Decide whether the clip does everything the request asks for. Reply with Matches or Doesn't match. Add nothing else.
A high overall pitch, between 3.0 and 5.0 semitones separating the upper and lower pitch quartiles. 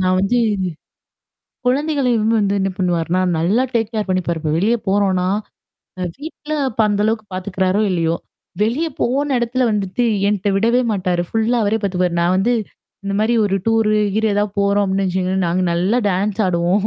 Matches